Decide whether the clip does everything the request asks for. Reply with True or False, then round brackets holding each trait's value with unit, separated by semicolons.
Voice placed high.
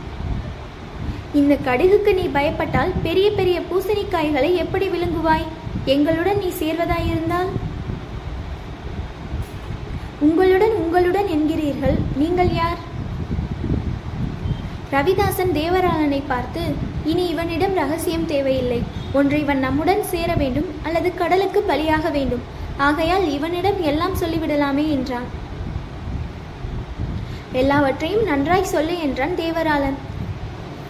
True (330 Hz)